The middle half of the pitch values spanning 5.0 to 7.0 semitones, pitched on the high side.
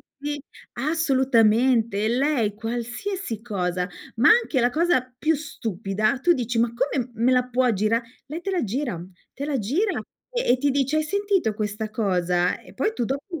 Yes: average, 5.3 semitones; very high, 250 Hz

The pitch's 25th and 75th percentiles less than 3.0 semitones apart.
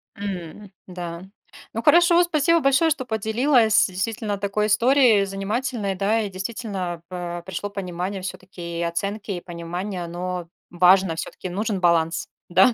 No: average, 3.8 semitones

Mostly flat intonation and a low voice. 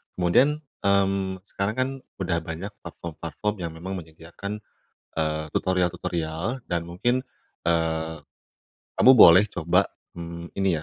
No: average, 3.1 semitones; very low, 90 Hz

